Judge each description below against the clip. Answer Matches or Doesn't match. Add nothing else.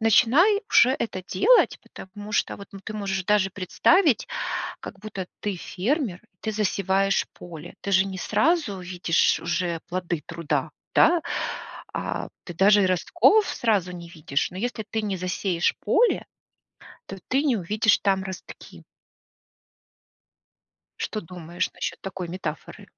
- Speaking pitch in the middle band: Doesn't match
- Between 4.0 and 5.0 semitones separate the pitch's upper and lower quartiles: Doesn't match